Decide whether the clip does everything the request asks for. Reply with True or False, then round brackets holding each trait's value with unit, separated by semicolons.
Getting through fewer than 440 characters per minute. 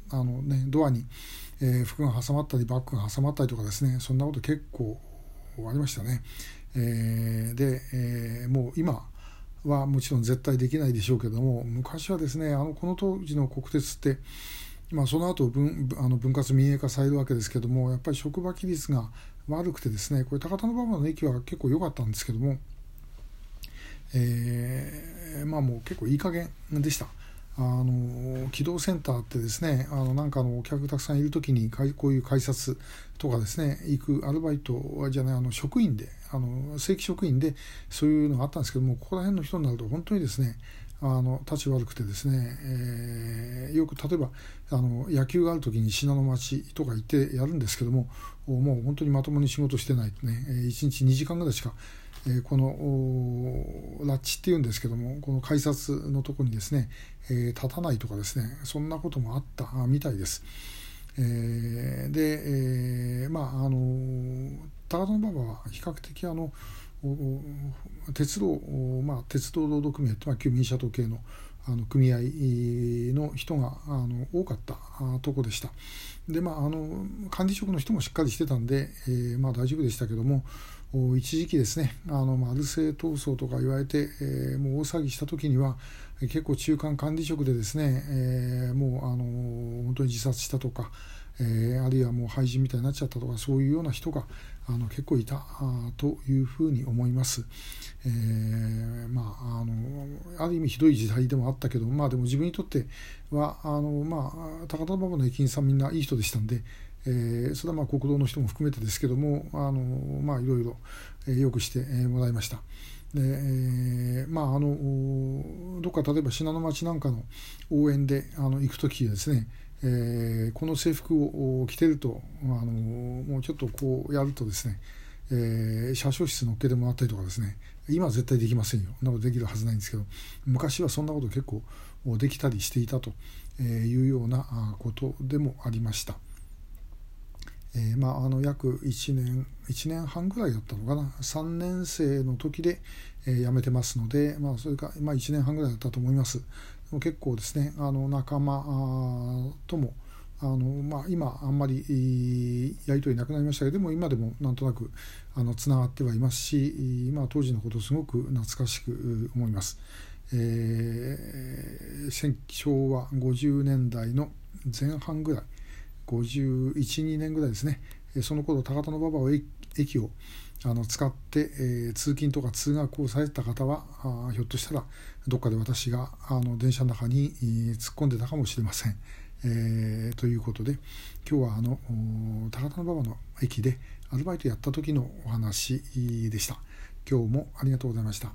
True (335 characters per minute)